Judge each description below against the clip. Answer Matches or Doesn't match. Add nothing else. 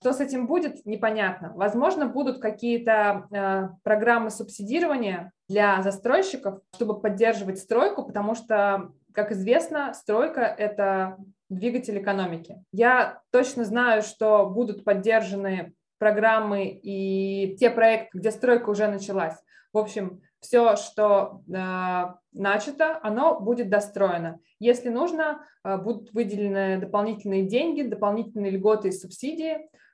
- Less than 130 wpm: Matches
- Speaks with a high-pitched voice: Matches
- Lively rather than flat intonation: Doesn't match